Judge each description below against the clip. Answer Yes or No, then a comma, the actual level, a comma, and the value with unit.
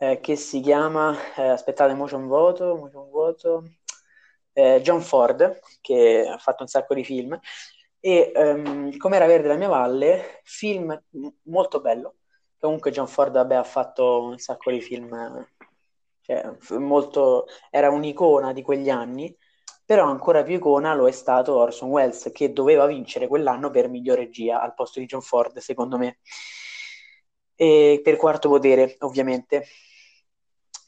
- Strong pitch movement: Yes, wide, 6.2 semitones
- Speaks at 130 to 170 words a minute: Yes, average, 145 wpm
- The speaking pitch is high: No, medium, 145 Hz